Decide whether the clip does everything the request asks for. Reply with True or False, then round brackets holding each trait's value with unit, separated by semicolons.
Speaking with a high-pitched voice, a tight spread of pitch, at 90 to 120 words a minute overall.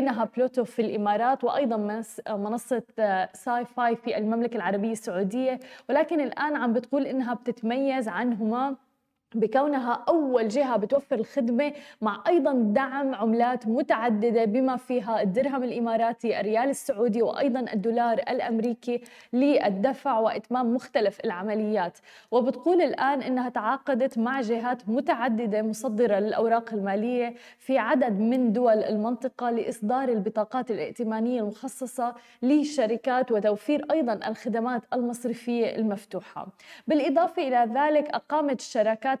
False (240 Hz; 3.0 semitones; 110 wpm)